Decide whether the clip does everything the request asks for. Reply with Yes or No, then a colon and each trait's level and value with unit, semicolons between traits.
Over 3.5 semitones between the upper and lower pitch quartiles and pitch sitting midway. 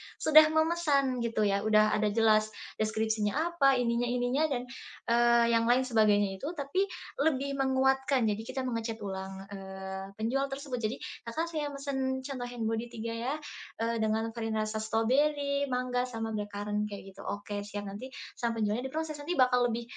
No: average, 3.9 semitones; high, 235 Hz